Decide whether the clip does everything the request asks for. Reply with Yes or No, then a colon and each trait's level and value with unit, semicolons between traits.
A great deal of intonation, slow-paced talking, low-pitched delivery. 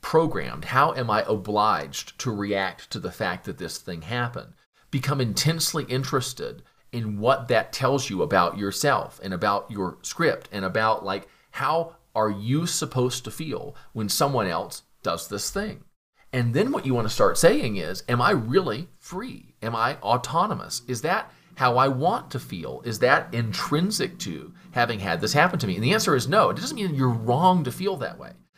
No: wide, 6.3 semitones; average, 190 wpm; low, 130 Hz